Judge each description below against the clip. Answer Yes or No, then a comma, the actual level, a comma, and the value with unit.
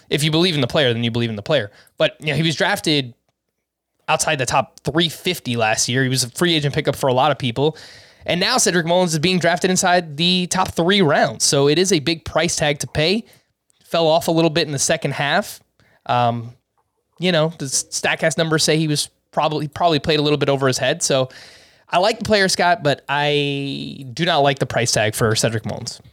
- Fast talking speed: Yes, fast, 230 wpm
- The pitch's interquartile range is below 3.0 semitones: No, average, 4.2 semitones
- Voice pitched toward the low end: No, medium, 155 Hz